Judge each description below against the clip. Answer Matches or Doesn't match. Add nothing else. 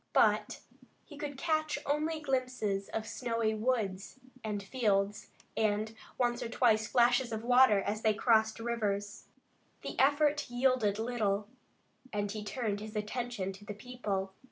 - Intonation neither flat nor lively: Matches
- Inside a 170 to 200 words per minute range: Doesn't match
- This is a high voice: Matches